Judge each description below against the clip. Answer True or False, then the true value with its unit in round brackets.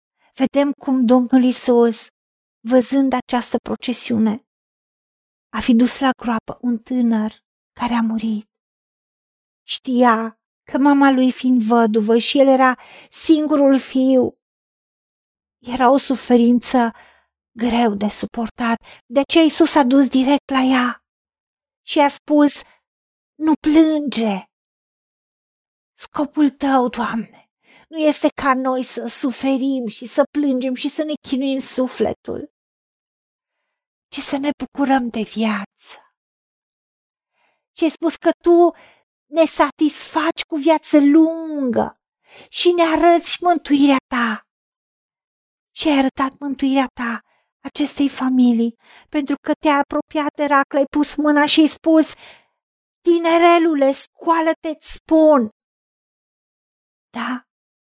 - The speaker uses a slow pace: True (110 wpm)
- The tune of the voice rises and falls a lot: False (3.7 semitones)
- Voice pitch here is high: True (270 Hz)